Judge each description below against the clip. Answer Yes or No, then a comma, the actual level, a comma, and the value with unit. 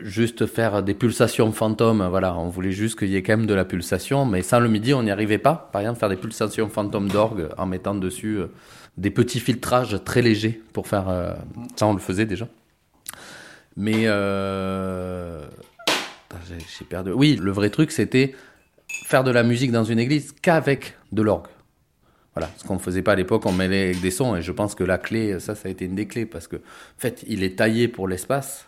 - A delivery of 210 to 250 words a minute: Yes, fast, 220 wpm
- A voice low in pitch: Yes, low, 105 Hz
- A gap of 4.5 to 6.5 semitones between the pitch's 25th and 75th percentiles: No, average, 3.6 semitones